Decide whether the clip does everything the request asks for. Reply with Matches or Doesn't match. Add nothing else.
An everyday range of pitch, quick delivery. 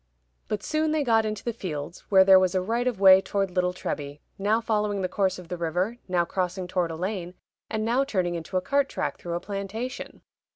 Matches